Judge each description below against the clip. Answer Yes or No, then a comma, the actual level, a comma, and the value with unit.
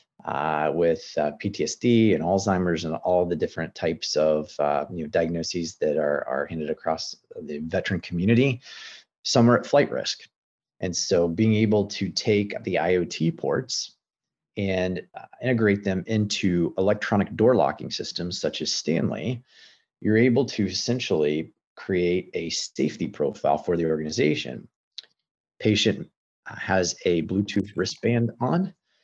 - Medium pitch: No, very low, 95 Hz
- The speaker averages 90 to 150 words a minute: Yes, slow, 135 wpm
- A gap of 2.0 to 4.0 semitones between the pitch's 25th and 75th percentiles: No, average, 4.5 semitones